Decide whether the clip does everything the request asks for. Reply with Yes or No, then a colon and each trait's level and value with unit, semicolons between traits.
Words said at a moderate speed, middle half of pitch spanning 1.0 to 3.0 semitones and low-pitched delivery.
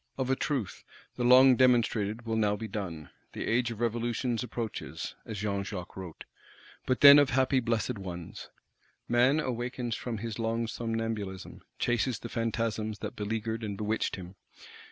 Yes: average, 155 wpm; narrow, 2.6 semitones; low, 115 Hz